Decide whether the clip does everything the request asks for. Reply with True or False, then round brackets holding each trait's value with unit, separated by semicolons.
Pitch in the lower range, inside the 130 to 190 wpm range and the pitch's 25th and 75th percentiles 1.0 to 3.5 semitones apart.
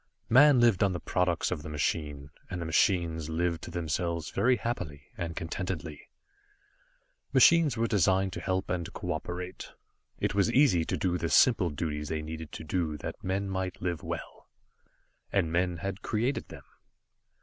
True (90 Hz; 160 wpm; 3.2 semitones)